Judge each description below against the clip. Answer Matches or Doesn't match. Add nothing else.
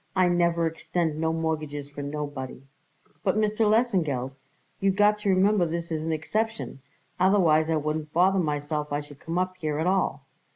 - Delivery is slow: Doesn't match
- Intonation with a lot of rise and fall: Doesn't match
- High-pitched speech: Doesn't match